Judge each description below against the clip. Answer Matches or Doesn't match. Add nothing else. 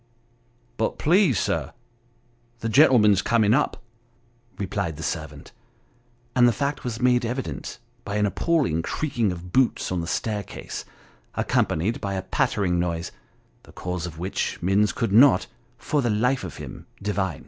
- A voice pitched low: Matches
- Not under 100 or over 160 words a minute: Matches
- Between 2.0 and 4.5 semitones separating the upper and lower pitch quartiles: Doesn't match